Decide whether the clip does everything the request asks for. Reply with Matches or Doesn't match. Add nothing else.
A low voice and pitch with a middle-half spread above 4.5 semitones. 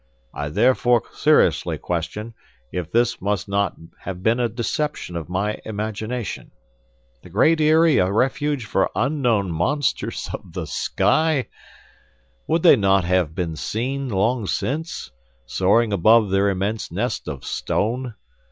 Matches